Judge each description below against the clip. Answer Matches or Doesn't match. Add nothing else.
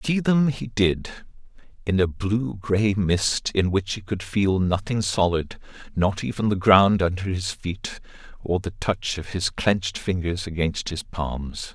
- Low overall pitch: Matches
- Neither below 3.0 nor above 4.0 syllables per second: Matches